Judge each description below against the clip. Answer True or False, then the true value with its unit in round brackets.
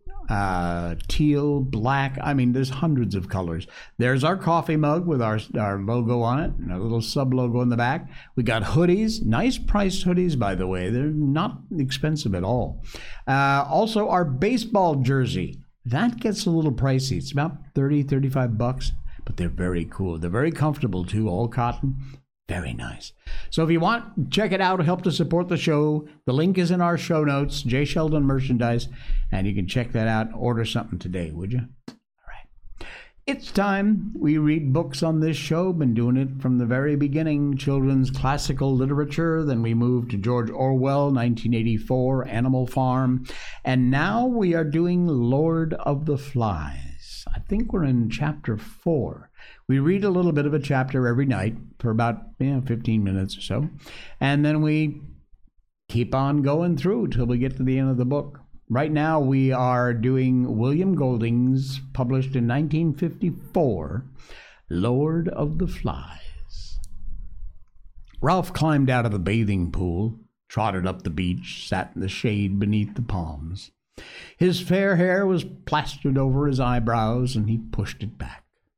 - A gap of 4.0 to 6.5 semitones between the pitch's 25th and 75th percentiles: True (5.3 semitones)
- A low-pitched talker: True (130 Hz)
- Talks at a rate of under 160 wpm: False (170 wpm)